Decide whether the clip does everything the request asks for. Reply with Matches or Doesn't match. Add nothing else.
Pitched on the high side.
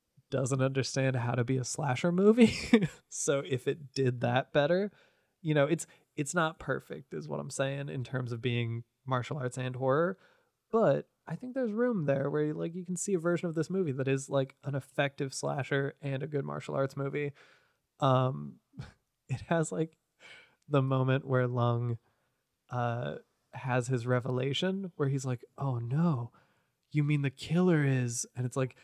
Doesn't match